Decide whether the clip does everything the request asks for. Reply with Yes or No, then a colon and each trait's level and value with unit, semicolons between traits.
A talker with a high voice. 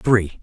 No: low, 105 Hz